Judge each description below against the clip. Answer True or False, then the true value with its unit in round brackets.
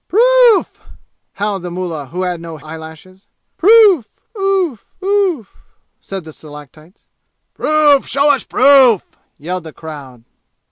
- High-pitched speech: True (195 Hz)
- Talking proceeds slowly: True (125 wpm)